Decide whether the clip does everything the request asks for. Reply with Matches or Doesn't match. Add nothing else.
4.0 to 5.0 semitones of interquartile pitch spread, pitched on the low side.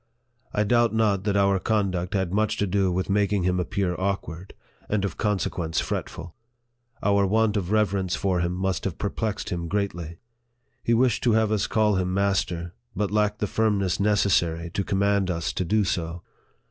Doesn't match